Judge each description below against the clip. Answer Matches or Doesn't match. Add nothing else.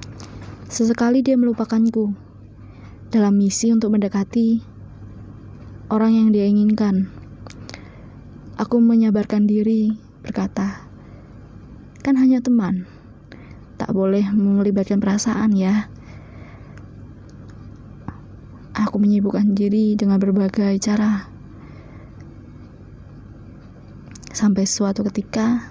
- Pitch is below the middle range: Doesn't match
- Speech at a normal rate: Doesn't match